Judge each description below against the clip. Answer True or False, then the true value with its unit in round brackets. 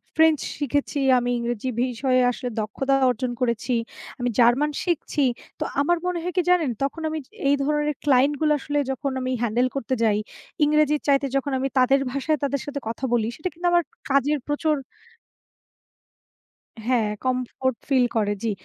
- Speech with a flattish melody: False (3.2 semitones)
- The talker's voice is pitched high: True (275 Hz)